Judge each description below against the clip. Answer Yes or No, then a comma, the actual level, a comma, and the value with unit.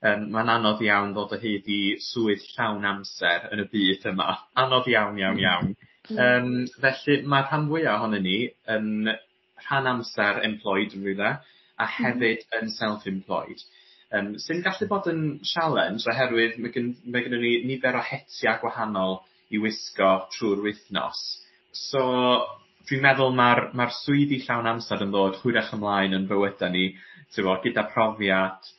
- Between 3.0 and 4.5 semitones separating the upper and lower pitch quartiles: Yes, average, 3.6 semitones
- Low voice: Yes, low, 110 Hz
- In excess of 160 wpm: No, average, 155 wpm